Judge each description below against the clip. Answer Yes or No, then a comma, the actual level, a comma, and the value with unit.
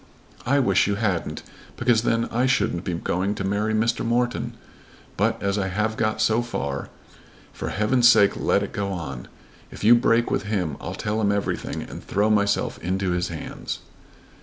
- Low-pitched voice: Yes, low, 105 Hz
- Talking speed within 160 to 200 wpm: Yes, average, 180 wpm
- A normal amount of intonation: Yes, average, 3.2 semitones